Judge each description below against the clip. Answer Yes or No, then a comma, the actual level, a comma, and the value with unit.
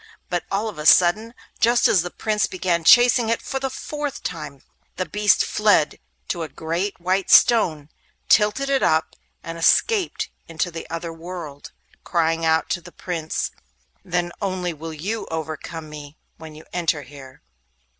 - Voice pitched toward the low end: No, medium, 175 Hz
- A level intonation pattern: No, average, 4.7 semitones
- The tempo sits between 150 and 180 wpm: Yes, average, 160 wpm